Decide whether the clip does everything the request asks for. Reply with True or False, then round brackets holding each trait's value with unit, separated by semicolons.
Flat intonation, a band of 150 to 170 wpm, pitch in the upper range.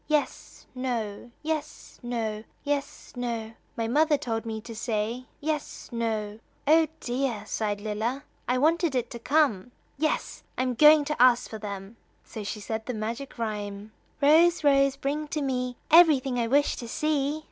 False (4.7 semitones; 160 wpm; 250 Hz)